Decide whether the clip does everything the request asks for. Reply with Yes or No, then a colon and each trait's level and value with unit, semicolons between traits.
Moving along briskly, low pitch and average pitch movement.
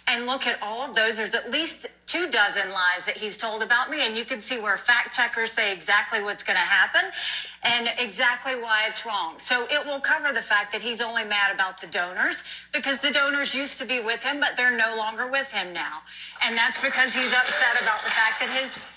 No: fast, 230 wpm; high, 240 Hz; average, 3.3 semitones